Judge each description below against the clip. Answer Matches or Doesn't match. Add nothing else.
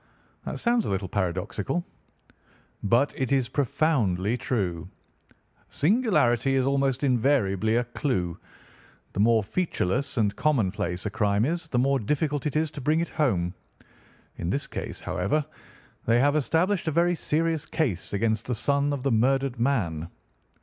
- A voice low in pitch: Matches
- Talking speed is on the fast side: Doesn't match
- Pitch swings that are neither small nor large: Doesn't match